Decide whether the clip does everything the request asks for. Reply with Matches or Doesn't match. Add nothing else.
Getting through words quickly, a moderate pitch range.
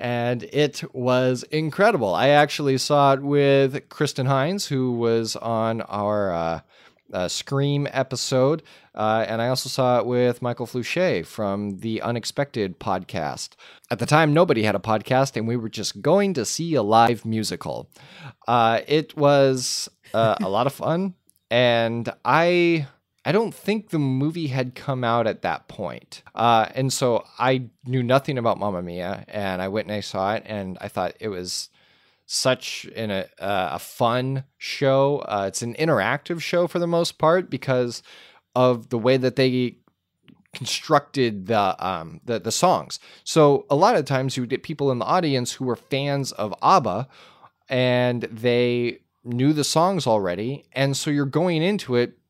Doesn't match